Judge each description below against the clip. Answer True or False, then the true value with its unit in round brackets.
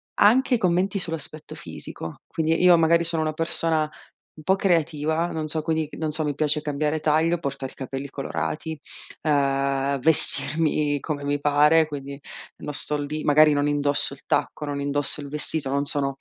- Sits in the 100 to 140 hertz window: False (150 Hz)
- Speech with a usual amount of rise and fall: False (2.1 semitones)